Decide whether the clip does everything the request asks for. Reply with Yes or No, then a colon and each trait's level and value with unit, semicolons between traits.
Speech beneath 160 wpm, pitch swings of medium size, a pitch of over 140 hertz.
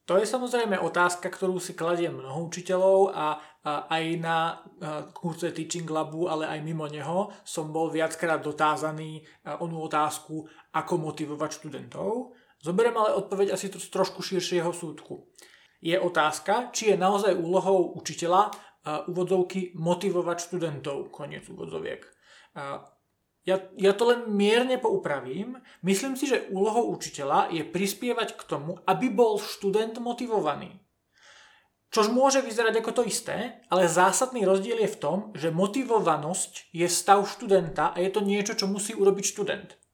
Yes: average, 145 wpm; average, 4.1 semitones; medium, 185 Hz